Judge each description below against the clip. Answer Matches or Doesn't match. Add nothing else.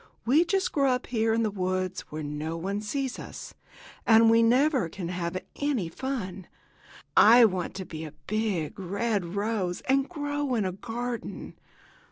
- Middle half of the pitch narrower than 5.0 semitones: Doesn't match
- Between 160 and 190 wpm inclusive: Matches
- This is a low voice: Doesn't match